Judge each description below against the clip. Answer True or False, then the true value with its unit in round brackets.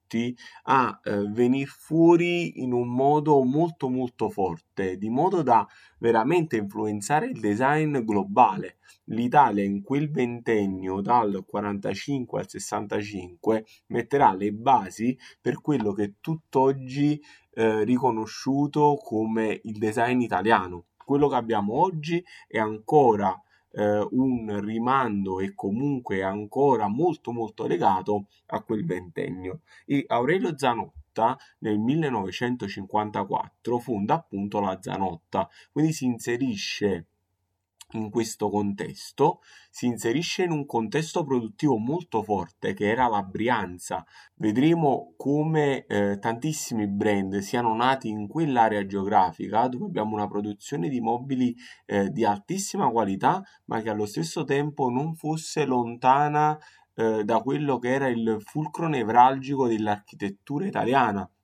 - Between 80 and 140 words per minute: True (120 wpm)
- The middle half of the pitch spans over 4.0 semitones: True (5.1 semitones)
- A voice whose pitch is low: True (115 Hz)